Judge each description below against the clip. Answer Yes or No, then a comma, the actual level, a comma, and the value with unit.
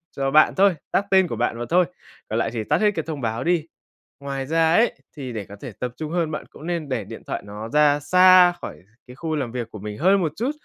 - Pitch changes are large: Yes, wide, 6.2 semitones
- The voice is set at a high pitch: No, medium, 150 Hz